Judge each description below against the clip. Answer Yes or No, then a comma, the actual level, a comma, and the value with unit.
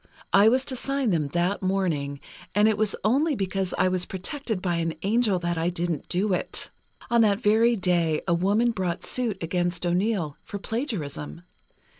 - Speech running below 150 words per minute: No, average, 175 wpm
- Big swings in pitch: No, average, 4.2 semitones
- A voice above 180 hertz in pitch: Yes, high, 190 Hz